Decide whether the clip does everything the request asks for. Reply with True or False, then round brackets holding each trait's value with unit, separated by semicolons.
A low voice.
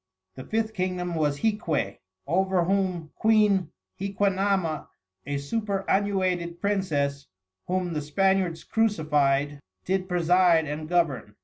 False (180 Hz)